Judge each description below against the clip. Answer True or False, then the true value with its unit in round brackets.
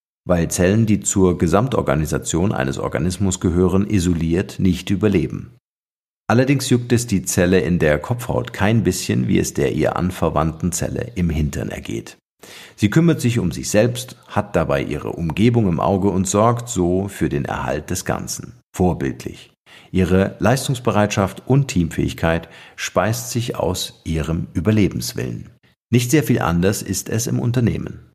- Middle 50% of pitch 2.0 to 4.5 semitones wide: False (5.0 semitones)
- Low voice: True (100 Hz)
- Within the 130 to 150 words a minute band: True (145 wpm)